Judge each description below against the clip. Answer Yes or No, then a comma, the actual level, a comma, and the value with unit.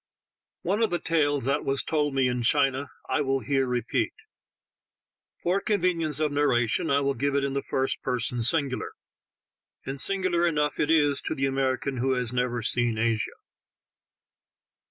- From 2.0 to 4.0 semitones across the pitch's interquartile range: Yes, average, 3.0 semitones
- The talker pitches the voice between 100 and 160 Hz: Yes, medium, 140 Hz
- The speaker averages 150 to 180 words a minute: Yes, average, 160 wpm